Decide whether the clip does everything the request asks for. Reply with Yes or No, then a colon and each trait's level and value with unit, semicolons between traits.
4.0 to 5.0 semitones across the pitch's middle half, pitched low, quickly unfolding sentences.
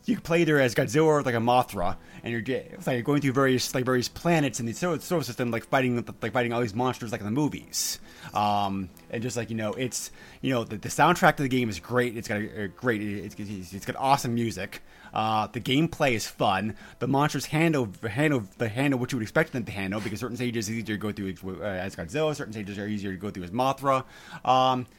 Yes: average, 4.4 semitones; low, 120 Hz; fast, 245 wpm